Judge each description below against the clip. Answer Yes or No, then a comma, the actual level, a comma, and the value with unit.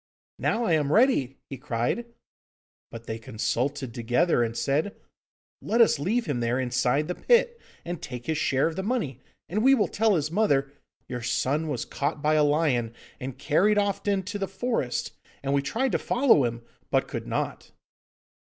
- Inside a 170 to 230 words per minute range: Yes, average, 180 wpm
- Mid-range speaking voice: Yes, medium, 150 Hz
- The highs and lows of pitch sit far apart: Yes, wide, 8.4 semitones